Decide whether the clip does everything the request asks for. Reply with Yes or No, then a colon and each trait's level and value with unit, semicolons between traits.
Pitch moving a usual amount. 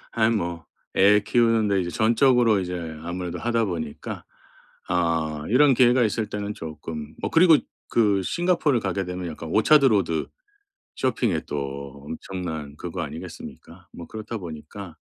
No: wide, 5.7 semitones